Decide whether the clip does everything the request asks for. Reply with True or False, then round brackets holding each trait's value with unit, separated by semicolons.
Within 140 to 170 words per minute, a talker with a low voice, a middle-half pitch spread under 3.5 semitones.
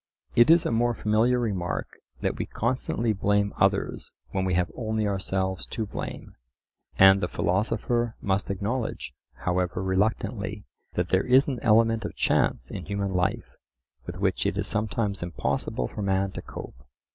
True (155 wpm; 100 Hz; 3.1 semitones)